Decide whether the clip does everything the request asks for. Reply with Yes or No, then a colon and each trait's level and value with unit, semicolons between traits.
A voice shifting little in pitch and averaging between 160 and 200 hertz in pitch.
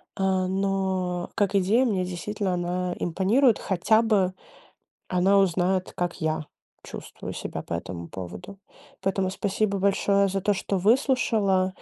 Yes: narrow, 1.8 semitones; high, 190 Hz